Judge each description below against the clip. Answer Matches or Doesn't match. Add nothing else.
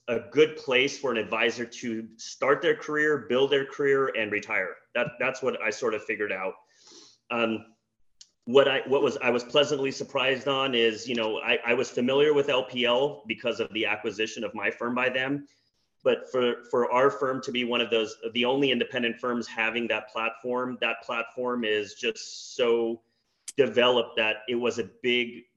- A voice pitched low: Matches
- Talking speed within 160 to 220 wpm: Matches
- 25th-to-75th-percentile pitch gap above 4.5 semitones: Doesn't match